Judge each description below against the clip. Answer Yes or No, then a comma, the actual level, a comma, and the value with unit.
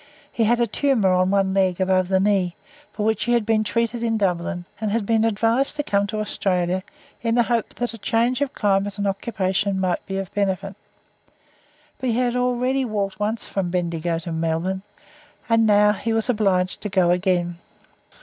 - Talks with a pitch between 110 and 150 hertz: No, high, 205 Hz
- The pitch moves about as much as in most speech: Yes, average, 3.4 semitones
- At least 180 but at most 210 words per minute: Yes, average, 190 wpm